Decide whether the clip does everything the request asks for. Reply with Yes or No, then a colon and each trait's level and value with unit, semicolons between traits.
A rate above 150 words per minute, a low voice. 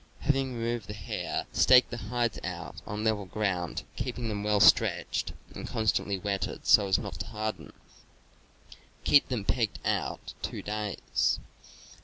No: average, 145 wpm; low, 105 Hz